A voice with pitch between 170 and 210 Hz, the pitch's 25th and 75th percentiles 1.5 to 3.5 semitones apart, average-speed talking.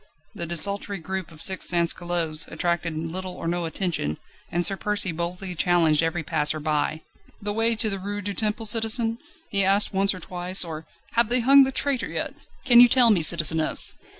No: medium, 185 Hz; average, 4.0 semitones; average, 185 wpm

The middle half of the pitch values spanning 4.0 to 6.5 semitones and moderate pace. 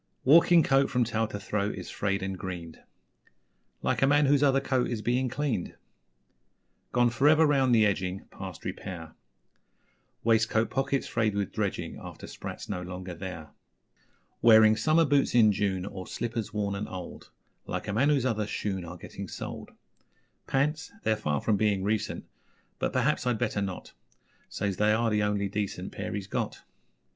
Yes: average, 4.7 semitones; average, 170 wpm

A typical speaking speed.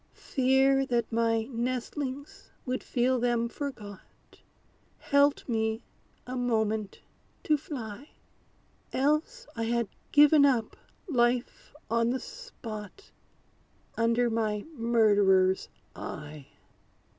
No: slow, 95 wpm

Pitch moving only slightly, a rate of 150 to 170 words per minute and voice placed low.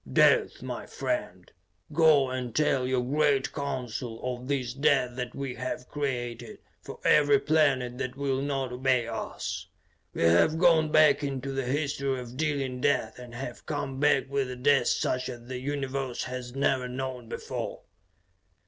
Yes: narrow, 2.2 semitones; average, 155 wpm; low, 130 Hz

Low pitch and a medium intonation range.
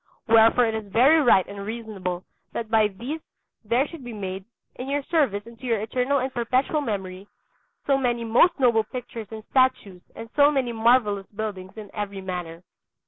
No: high, 225 Hz; average, 4.1 semitones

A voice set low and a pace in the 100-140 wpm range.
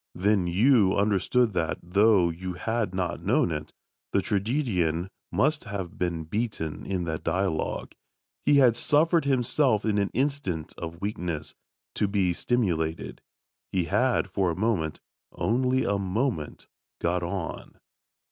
Yes: low, 100 Hz; slow, 135 wpm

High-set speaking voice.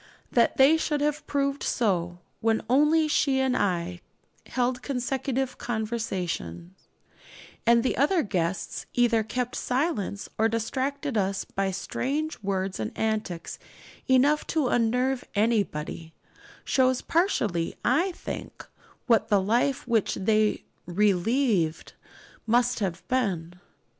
Yes: high, 230 Hz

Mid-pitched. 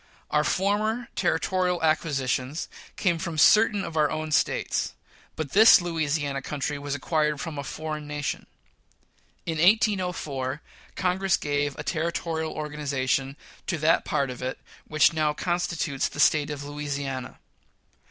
Yes: medium, 155 Hz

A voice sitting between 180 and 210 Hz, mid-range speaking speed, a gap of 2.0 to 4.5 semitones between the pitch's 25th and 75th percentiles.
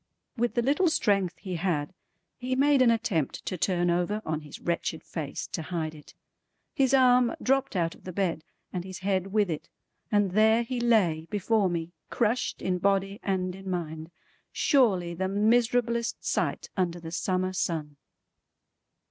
No: high, 190 Hz; average, 165 wpm; average, 5.2 semitones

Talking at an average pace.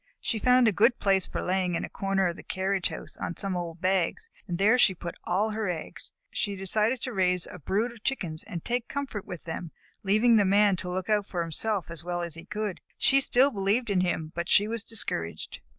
No: fast, 230 wpm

